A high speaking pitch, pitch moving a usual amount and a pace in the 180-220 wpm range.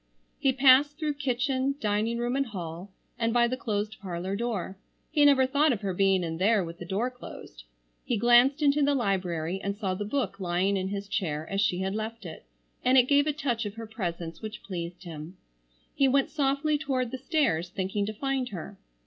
No: high, 220 Hz; wide, 5.9 semitones; fast, 205 wpm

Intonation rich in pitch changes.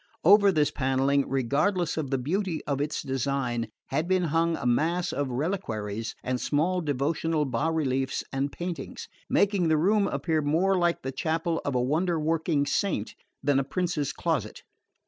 No: average, 4.3 semitones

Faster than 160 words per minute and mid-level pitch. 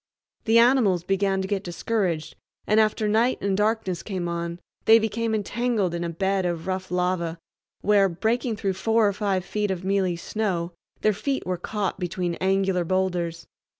No: average, 170 wpm; high, 195 Hz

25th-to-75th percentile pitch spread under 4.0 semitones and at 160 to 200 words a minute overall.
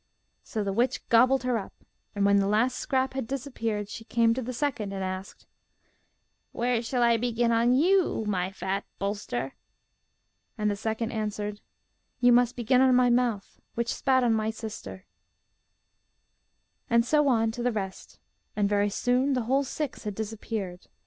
Yes: average, 3.3 semitones; average, 165 wpm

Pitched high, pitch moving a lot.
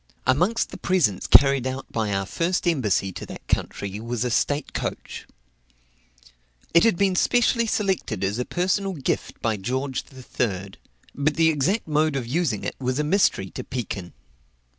No: low, 135 Hz; wide, 7.8 semitones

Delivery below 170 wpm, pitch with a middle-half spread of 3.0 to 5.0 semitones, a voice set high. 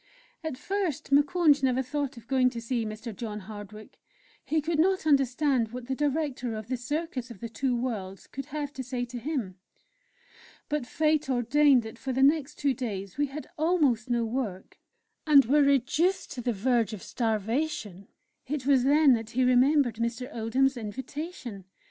No: average, 175 wpm; average, 4.0 semitones; very high, 255 Hz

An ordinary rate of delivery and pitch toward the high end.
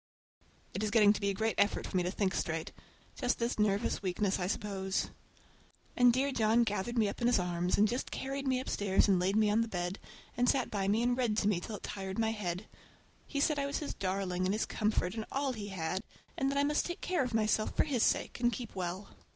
No: fast, 245 wpm; high, 215 Hz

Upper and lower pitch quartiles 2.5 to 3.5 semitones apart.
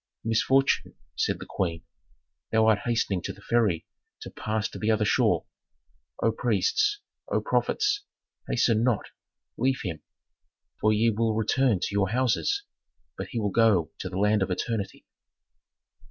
Yes: average, 2.9 semitones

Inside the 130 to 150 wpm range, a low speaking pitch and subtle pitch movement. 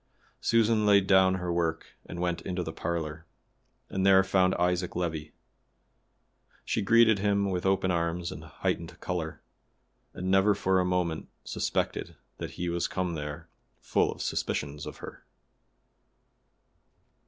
Yes: average, 140 wpm; very low, 90 Hz; narrow, 2.3 semitones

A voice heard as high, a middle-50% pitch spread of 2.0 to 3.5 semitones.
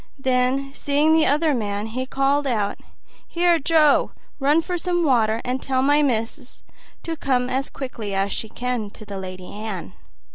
No: very high, 260 Hz; average, 4.8 semitones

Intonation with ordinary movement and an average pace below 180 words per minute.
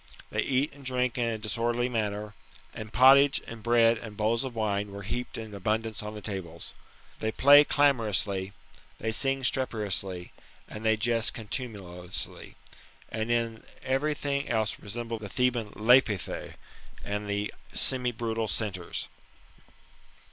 Yes: average, 3.1 semitones; average, 140 wpm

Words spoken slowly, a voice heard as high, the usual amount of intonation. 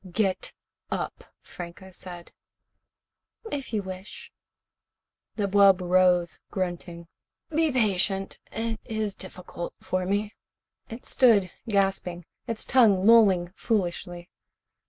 Yes: slow, 100 wpm; high, 195 Hz; average, 3.2 semitones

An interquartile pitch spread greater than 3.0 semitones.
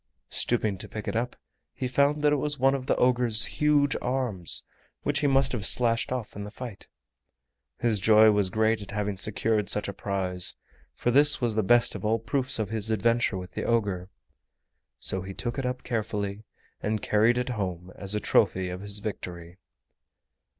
Yes: average, 3.7 semitones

